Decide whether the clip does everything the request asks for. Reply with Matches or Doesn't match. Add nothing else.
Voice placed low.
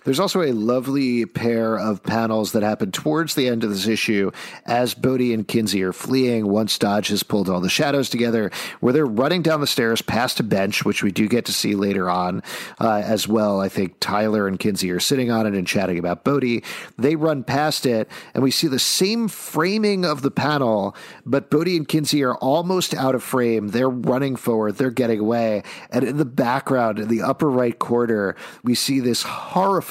Matches